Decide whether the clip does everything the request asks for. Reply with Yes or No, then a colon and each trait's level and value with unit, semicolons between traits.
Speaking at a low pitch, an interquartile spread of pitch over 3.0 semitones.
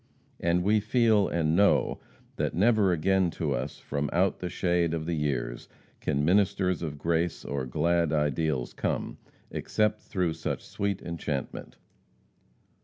Yes: very low, 85 Hz; average, 3.9 semitones